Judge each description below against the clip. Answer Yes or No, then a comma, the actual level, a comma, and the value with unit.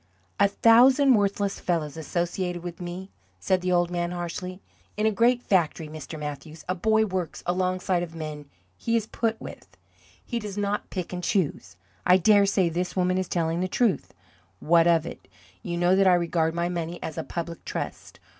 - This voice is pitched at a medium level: Yes, medium, 180 Hz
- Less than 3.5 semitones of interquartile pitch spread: Yes, average, 2.8 semitones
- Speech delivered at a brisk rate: No, average, 190 wpm